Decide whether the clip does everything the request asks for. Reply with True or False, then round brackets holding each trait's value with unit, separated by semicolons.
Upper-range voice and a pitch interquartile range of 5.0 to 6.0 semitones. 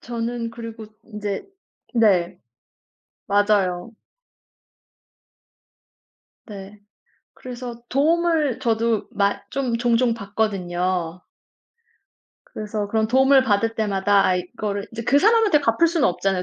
False (220 Hz; 3.4 semitones)